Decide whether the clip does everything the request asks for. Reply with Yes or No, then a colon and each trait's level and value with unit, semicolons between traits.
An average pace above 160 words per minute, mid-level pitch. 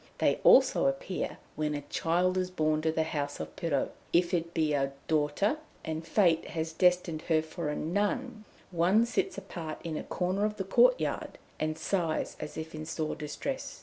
Yes: average, 180 wpm; medium, 165 Hz